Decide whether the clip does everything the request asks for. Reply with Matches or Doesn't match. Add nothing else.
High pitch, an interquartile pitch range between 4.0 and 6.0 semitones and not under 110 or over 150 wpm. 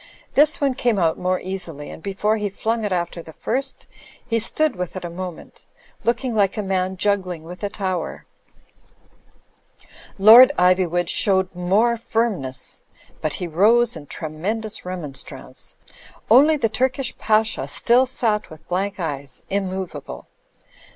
Matches